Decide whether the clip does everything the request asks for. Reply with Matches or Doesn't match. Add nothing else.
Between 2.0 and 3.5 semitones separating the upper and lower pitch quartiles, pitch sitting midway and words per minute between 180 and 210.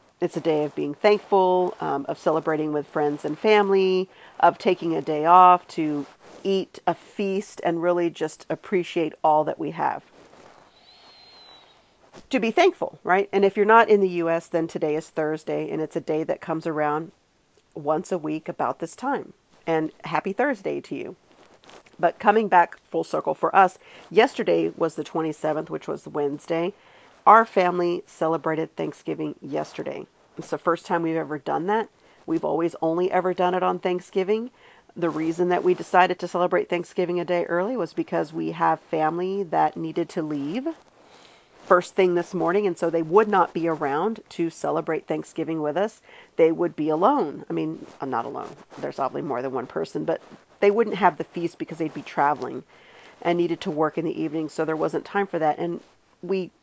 Matches